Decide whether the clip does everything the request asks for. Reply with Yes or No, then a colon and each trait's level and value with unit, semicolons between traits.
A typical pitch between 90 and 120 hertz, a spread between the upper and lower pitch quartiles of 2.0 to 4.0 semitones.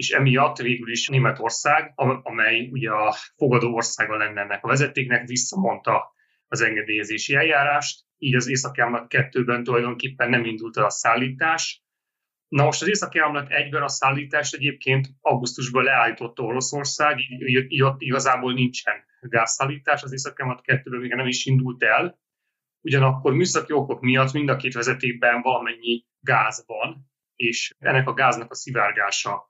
No: low, 130 Hz; average, 2.9 semitones